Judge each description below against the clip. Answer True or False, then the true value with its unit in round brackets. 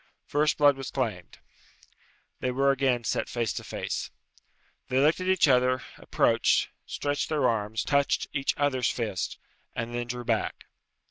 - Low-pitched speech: True (130 Hz)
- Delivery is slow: False (150 wpm)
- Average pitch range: True (3.1 semitones)